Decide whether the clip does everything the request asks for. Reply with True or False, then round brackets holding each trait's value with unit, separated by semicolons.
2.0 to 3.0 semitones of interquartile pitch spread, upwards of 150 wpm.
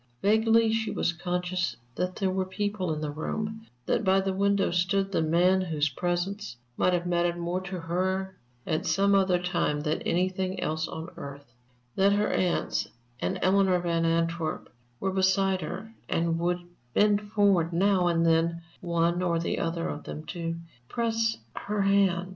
True (2.7 semitones; 165 wpm)